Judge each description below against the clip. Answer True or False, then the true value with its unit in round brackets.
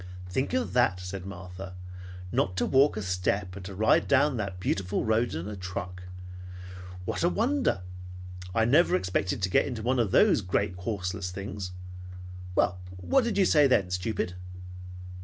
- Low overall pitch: True (100 Hz)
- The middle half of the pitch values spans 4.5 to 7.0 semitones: True (5.2 semitones)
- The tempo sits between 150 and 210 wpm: True (165 wpm)